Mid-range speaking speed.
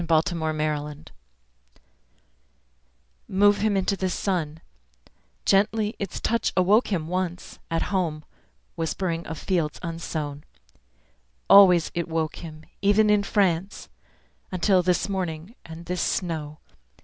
No: slow, 115 wpm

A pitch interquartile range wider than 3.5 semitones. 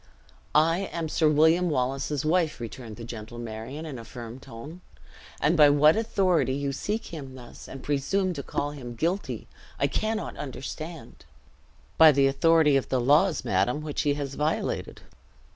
Yes: average, 3.9 semitones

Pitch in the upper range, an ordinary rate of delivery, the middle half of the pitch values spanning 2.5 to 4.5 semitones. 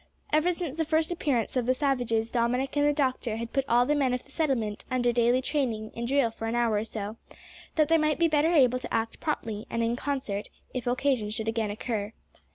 No: very high, 250 Hz; fast, 225 wpm; average, 4.2 semitones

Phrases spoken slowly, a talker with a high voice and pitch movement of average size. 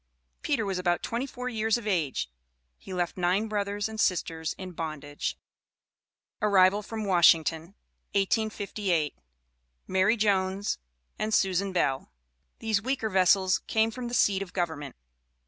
Yes: slow, 130 wpm; high, 195 Hz; average, 3.5 semitones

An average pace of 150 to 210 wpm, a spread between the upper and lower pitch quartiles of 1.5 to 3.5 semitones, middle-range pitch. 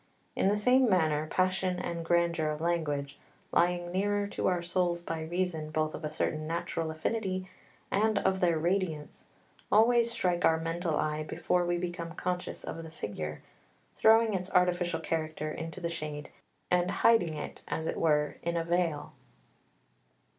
Yes: average, 160 wpm; average, 2.7 semitones; medium, 170 Hz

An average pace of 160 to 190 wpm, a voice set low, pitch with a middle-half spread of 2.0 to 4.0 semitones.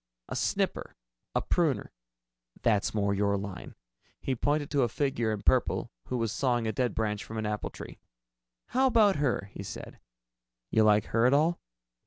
No: average, 175 wpm; low, 115 Hz; average, 4.9 semitones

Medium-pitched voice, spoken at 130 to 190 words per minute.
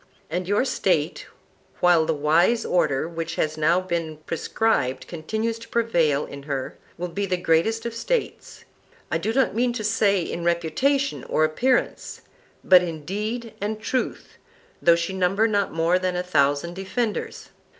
Yes: medium, 180 Hz; average, 160 wpm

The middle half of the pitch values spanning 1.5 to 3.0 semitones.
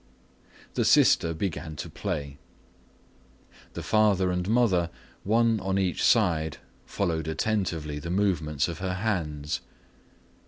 No: average, 4.2 semitones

